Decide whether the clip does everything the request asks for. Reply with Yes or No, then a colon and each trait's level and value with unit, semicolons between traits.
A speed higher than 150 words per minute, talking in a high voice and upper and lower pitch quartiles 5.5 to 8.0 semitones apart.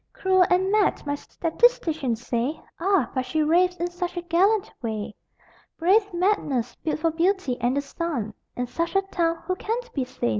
Yes: average, 180 wpm; very high, 335 Hz; wide, 6.0 semitones